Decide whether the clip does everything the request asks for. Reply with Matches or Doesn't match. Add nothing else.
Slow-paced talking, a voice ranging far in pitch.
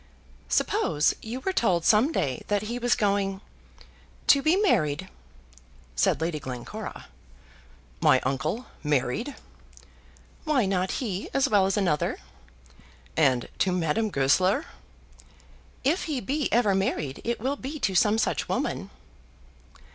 Matches